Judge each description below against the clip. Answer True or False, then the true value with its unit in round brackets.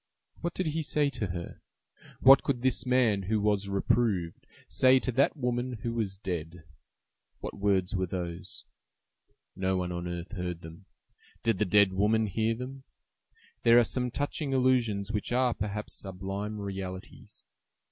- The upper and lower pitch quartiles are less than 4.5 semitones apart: False (4.9 semitones)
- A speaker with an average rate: True (155 wpm)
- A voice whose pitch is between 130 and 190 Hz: False (105 Hz)